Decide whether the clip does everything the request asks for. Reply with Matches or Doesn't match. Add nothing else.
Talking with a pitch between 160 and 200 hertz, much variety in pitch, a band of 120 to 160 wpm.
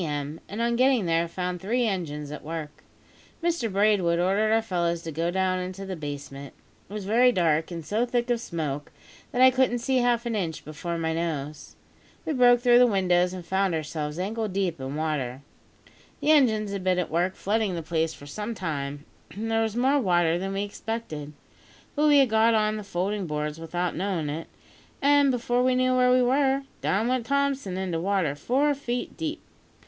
Doesn't match